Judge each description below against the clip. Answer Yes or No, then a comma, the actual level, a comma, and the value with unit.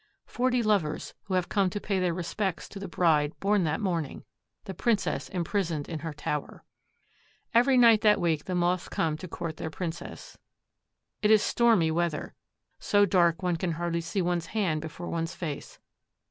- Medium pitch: Yes, medium, 175 Hz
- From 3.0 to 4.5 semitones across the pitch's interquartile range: Yes, average, 3.6 semitones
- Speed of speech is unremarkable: Yes, average, 170 wpm